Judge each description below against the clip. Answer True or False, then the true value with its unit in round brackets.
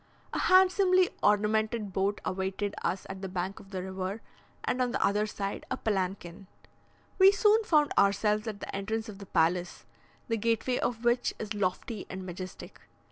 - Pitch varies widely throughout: False (3.3 semitones)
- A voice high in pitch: True (205 Hz)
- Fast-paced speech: False (170 wpm)